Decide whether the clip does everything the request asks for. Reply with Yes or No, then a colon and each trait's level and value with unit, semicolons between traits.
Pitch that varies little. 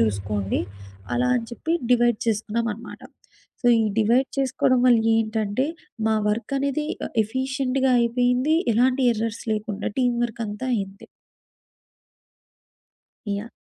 No: average, 3.3 semitones